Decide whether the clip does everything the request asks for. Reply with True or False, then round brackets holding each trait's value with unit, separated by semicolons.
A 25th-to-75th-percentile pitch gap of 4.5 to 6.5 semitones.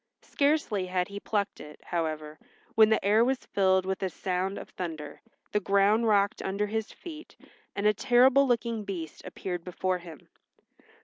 False (3.5 semitones)